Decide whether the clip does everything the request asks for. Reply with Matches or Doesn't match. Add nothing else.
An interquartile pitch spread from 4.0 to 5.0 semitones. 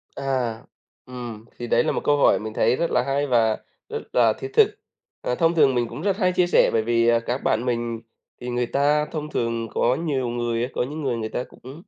Doesn't match